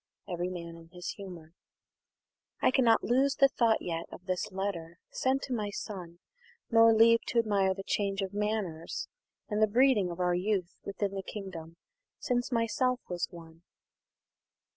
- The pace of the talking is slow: No, average, 160 wpm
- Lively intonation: No, average, 4.3 semitones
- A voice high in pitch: Yes, high, 195 Hz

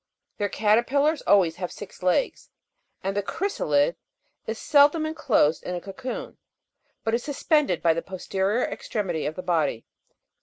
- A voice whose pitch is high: Yes, high, 200 Hz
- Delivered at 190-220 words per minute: No, average, 145 wpm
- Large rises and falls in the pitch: Yes, wide, 7.0 semitones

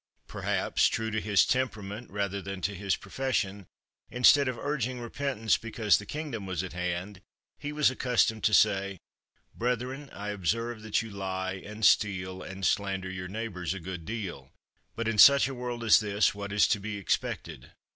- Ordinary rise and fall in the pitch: Yes, average, 3.6 semitones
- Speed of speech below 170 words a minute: No, average, 175 wpm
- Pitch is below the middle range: Yes, low, 105 Hz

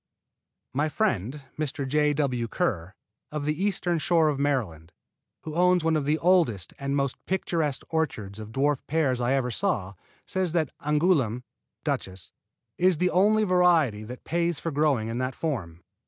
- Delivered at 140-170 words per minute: Yes, average, 160 wpm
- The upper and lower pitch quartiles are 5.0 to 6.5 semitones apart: Yes, wide, 5.4 semitones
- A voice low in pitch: No, medium, 145 Hz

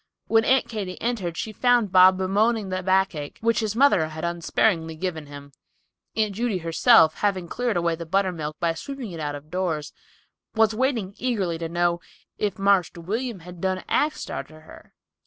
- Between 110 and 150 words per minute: No, average, 170 wpm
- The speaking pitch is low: No, medium, 185 Hz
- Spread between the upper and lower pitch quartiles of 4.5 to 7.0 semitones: Yes, average, 4.9 semitones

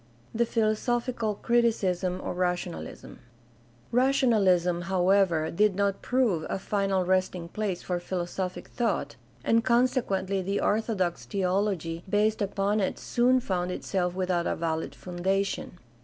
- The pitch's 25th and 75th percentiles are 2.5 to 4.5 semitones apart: Yes, average, 3.3 semitones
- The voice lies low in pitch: No, high, 190 Hz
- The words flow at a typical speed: No, slow, 125 wpm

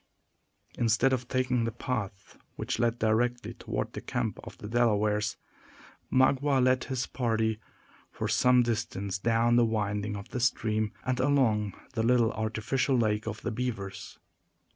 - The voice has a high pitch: No, low, 115 Hz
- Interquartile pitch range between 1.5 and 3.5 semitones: Yes, narrow, 2.6 semitones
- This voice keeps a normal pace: Yes, average, 145 wpm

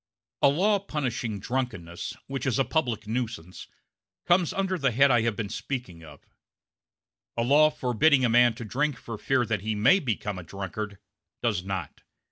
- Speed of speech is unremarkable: Yes, average, 170 wpm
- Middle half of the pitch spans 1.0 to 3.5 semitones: No, average, 5.0 semitones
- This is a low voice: Yes, low, 120 Hz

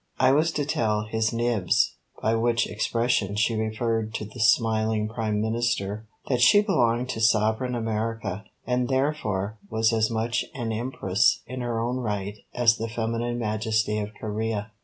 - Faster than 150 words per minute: Yes, average, 160 wpm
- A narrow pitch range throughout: Yes, narrow, 1.9 semitones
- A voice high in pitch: No, low, 110 Hz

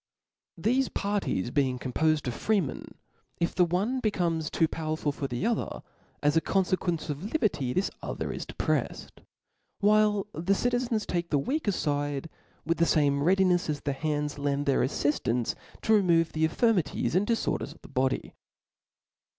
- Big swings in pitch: Yes, wide, 5.8 semitones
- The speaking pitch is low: No, medium, 165 Hz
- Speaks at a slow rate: No, average, 160 wpm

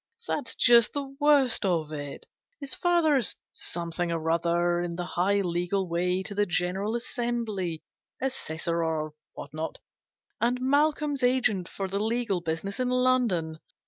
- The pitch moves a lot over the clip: Yes, wide, 6.8 semitones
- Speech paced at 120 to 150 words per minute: Yes, average, 145 wpm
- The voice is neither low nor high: No, high, 195 Hz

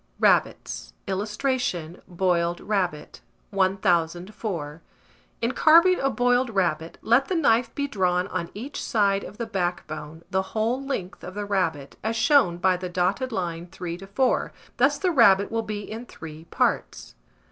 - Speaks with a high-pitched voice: Yes, high, 195 Hz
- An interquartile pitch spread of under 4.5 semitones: No, average, 4.8 semitones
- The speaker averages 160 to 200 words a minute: No, average, 150 wpm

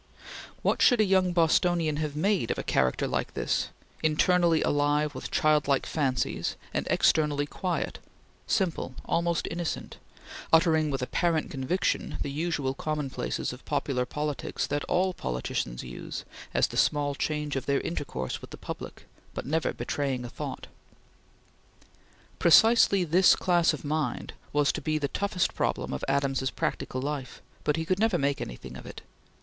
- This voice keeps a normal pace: Yes, average, 155 wpm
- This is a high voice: No, medium, 150 Hz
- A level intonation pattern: No, average, 3.7 semitones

